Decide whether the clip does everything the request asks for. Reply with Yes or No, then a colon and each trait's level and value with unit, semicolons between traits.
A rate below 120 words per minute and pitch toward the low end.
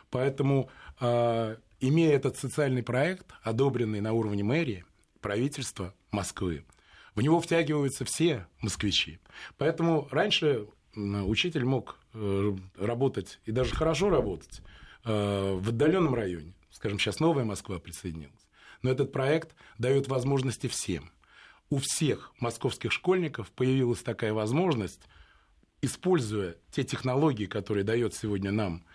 Yes: slow, 110 wpm; low, 120 Hz